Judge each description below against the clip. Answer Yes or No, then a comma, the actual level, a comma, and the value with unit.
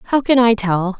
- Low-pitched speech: No, high, 220 Hz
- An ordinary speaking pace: No, fast, 240 wpm